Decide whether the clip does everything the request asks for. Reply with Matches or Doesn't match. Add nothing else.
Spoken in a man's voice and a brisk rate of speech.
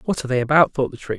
Matches